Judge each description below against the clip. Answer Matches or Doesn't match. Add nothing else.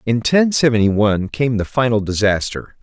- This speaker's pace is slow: Doesn't match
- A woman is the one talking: Doesn't match